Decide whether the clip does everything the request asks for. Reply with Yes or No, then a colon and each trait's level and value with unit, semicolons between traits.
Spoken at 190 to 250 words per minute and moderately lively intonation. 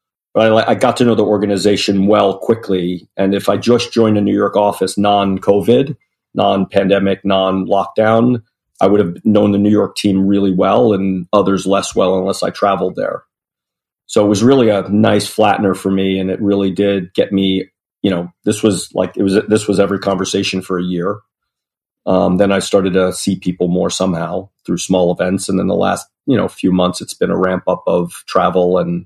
No: average, 195 wpm; narrow, 1.6 semitones